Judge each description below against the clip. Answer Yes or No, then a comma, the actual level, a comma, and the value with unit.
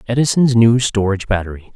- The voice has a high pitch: No, low, 110 Hz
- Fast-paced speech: No, slow, 135 wpm